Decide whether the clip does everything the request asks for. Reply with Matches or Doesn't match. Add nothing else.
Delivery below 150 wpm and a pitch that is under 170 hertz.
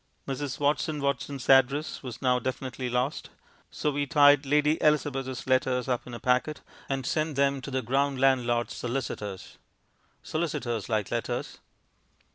Matches